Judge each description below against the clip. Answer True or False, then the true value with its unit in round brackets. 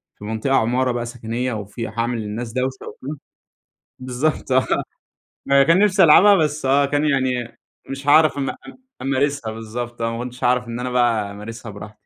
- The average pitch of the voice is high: False (125 Hz)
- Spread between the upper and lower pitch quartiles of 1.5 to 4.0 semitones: True (3.2 semitones)